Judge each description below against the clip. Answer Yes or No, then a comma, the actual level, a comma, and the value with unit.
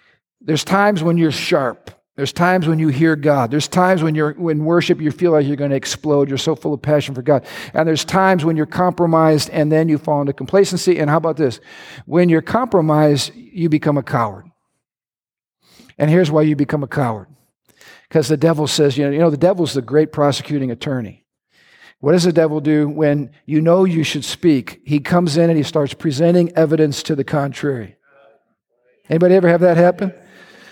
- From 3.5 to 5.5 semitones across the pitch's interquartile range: No, average, 2.9 semitones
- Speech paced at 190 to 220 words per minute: Yes, average, 200 wpm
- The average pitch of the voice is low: No, medium, 155 Hz